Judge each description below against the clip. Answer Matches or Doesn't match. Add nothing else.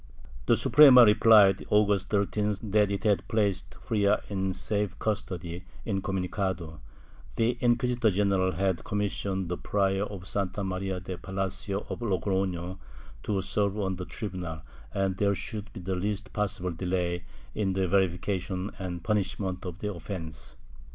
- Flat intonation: Matches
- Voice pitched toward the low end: Matches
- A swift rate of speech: Doesn't match